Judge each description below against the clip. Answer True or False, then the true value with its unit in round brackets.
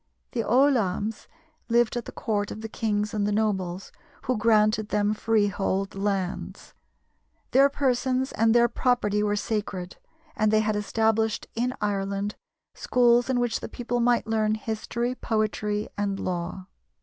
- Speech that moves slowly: False (145 wpm)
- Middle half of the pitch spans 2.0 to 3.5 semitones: True (2.5 semitones)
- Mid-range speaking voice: False (215 Hz)